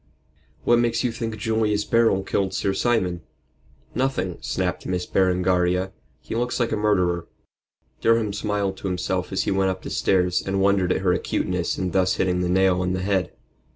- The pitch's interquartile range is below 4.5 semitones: Yes, average, 2.8 semitones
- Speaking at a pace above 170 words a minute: Yes, average, 180 wpm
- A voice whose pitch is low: Yes, very low, 95 Hz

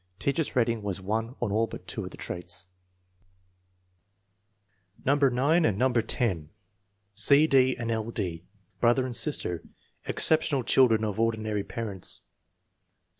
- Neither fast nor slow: No, slow, 130 wpm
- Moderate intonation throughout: Yes, average, 4.0 semitones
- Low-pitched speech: Yes, low, 115 Hz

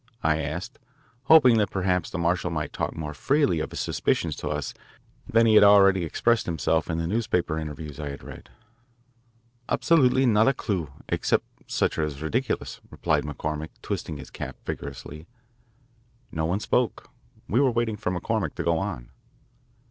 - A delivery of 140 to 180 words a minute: Yes, average, 165 wpm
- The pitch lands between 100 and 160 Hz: No, very low, 90 Hz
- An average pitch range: No, wide, 6.4 semitones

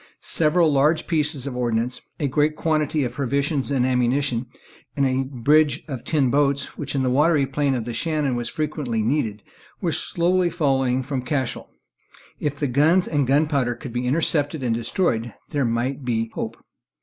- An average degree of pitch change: Yes, average, 3.2 semitones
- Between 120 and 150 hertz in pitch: Yes, medium, 140 Hz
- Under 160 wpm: No, average, 175 wpm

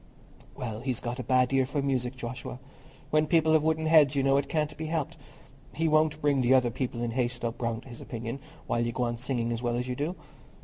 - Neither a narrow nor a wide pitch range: Yes, average, 3.7 semitones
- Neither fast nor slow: No, fast, 235 wpm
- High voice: No, low, 130 Hz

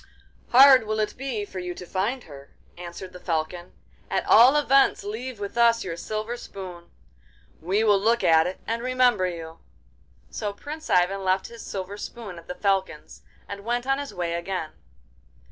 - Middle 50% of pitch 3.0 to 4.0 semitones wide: No, average, 4.8 semitones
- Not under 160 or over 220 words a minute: Yes, average, 175 wpm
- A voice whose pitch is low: No, high, 200 Hz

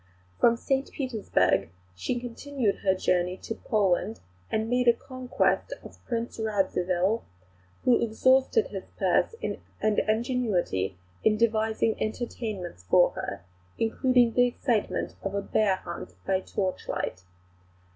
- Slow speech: Yes, slow, 120 wpm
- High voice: Yes, high, 220 Hz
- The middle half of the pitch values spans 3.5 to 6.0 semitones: Yes, average, 4.4 semitones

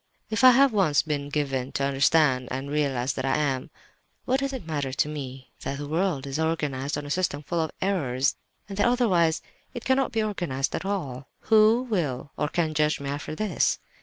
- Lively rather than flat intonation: Yes, wide, 6.1 semitones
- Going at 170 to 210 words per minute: Yes, average, 195 wpm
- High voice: No, medium, 150 Hz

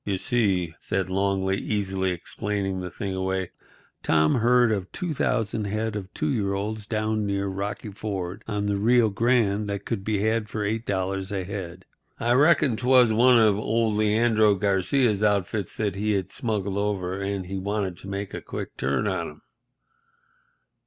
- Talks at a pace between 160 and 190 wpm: Yes, average, 165 wpm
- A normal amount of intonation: No, narrow, 2.3 semitones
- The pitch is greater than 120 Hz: No, low, 100 Hz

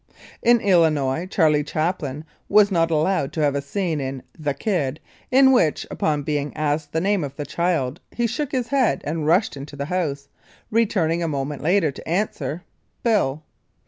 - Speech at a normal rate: Yes, average, 175 wpm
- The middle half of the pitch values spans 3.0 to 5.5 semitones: Yes, average, 4.9 semitones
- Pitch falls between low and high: Yes, medium, 160 Hz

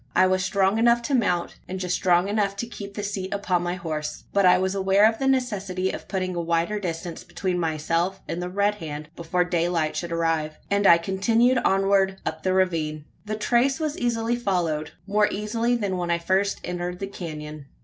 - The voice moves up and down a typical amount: Yes, average, 3.2 semitones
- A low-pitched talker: No, high, 190 Hz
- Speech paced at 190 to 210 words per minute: Yes, average, 200 wpm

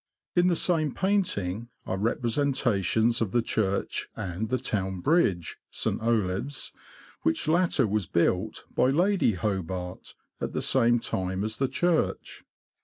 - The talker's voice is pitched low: Yes, low, 115 Hz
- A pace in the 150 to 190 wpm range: No, slow, 135 wpm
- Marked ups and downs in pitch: Yes, wide, 6.9 semitones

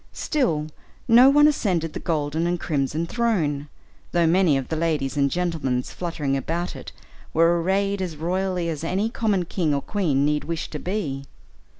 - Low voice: No, medium, 165 Hz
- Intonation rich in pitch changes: No, average, 4.1 semitones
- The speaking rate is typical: Yes, average, 170 wpm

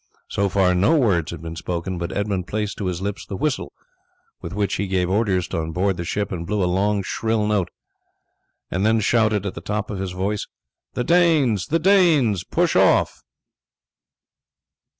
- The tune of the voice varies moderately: Yes, average, 3.0 semitones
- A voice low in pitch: Yes, low, 100 Hz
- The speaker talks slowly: No, average, 180 wpm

